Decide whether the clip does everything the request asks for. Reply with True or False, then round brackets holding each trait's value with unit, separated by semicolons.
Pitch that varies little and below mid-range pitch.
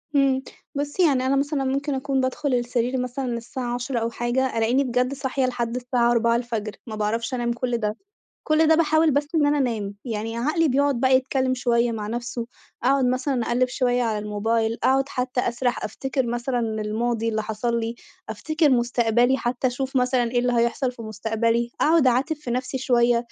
False (2.3 semitones; 245 Hz)